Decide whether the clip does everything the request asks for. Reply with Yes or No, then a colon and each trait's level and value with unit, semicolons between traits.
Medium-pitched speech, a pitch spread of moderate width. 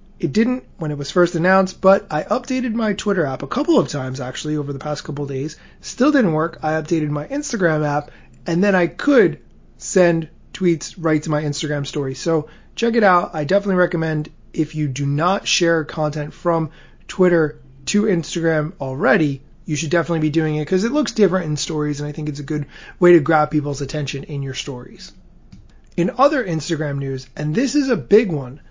Yes: medium, 160 Hz; average, 4.0 semitones